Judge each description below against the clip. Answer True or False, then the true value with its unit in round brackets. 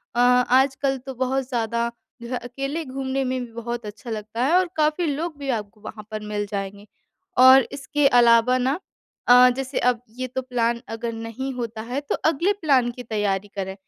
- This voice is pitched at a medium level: False (250 Hz)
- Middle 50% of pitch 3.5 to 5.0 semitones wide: False (2.9 semitones)